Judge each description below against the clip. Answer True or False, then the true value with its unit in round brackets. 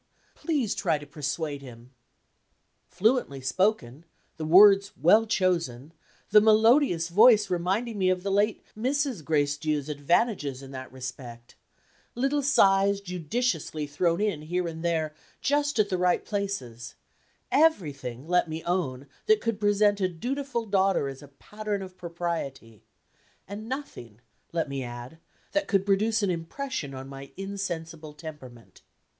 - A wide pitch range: True (6.5 semitones)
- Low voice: False (175 Hz)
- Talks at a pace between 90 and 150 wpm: True (140 wpm)